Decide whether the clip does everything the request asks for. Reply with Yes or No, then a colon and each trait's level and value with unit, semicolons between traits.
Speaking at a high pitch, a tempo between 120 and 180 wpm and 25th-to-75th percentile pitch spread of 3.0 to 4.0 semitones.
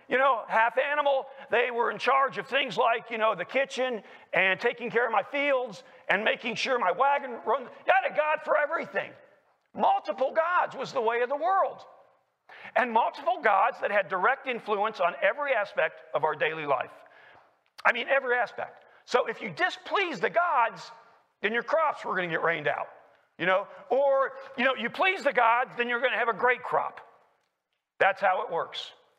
No: very high, 255 Hz; average, 195 wpm; average, 3.4 semitones